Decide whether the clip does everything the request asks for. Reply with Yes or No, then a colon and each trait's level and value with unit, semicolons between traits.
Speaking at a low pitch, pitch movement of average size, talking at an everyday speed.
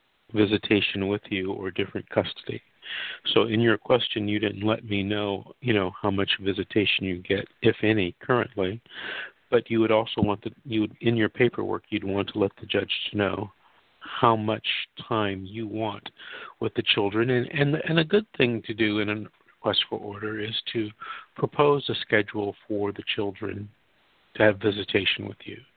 No: low, 105 Hz; narrow, 2.2 semitones; average, 180 wpm